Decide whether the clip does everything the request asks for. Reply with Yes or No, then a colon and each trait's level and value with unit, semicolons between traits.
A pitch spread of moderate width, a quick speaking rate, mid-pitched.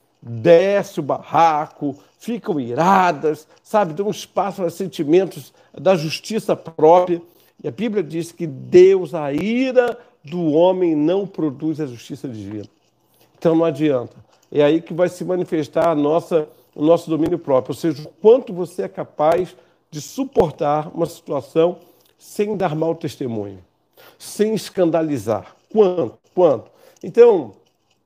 No: average, 3.7 semitones; average, 135 wpm; medium, 165 Hz